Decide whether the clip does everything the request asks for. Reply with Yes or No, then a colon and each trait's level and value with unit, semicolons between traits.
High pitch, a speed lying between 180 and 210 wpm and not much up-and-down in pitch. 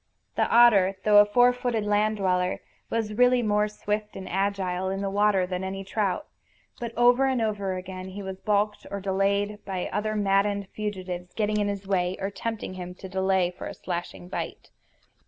Yes: high, 200 Hz; average, 185 wpm; narrow, 2.0 semitones